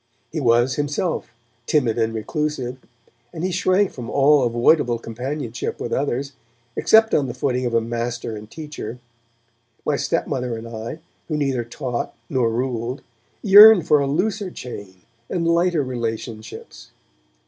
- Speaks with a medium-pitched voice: No, low, 130 Hz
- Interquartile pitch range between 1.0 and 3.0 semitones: No, average, 4.6 semitones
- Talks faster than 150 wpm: No, average, 140 wpm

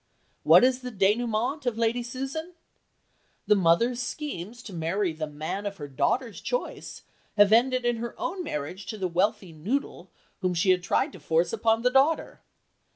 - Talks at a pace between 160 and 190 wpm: Yes, average, 170 wpm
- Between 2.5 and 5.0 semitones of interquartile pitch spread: No, wide, 5.5 semitones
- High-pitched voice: Yes, high, 220 Hz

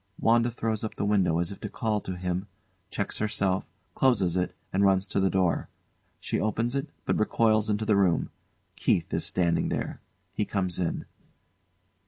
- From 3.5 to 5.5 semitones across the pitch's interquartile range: No, average, 2.8 semitones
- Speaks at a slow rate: No, average, 175 wpm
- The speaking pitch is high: No, low, 100 Hz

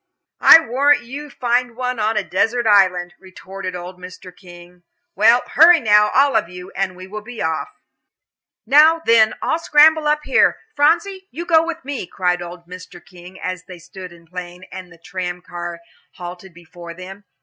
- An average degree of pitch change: No, wide, 6.1 semitones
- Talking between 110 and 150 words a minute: No, average, 180 wpm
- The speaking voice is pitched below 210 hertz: Yes, high, 190 Hz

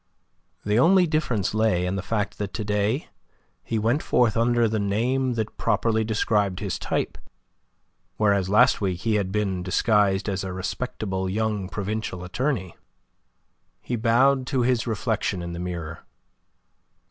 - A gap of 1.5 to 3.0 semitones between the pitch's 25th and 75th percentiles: No, average, 3.4 semitones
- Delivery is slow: No, average, 145 wpm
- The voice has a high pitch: No, low, 105 Hz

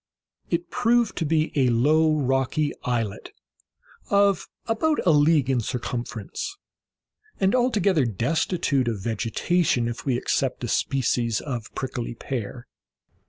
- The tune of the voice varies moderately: No, wide, 6.0 semitones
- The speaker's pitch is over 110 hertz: Yes, low, 135 Hz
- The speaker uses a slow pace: Yes, slow, 120 wpm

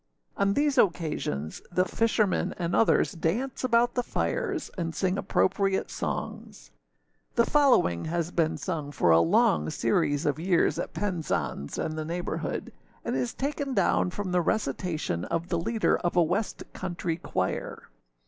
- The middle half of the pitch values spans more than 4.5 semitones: Yes, wide, 5.4 semitones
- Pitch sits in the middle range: Yes, medium, 175 Hz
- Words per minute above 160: No, average, 150 wpm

